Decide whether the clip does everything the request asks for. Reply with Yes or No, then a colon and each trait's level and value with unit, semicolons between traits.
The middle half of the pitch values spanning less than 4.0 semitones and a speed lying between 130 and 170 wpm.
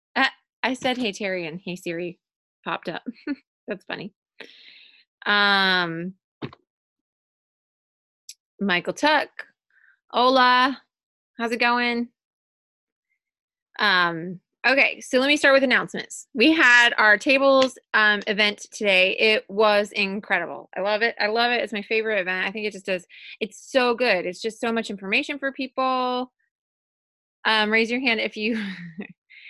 No: average, 4.5 semitones; slow, 135 wpm